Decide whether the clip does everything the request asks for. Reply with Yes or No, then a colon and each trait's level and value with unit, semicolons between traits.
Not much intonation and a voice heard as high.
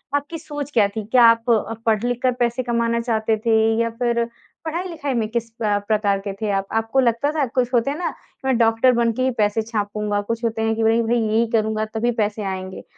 Yes: narrow, 2.0 semitones; high, 230 Hz